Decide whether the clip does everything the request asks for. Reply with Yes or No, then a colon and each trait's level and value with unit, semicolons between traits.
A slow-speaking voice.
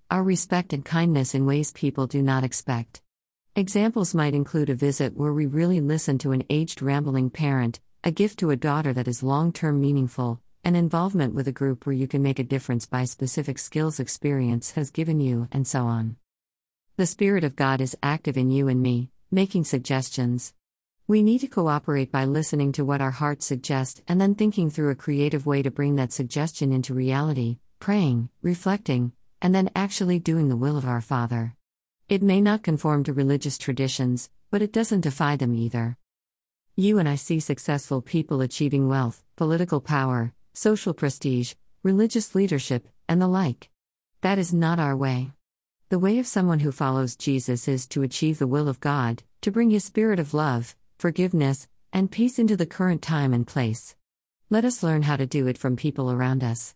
No: average, 185 wpm